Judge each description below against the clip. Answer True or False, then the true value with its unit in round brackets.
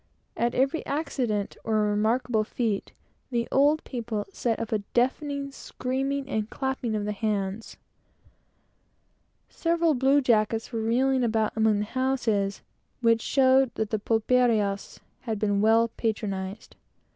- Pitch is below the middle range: False (230 Hz)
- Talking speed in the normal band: False (125 wpm)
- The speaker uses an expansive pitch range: False (3.5 semitones)